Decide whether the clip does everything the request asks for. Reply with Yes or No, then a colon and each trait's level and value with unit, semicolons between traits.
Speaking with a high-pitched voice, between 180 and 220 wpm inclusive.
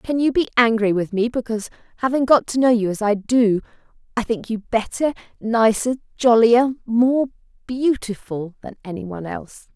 No: high, 230 Hz; average, 165 wpm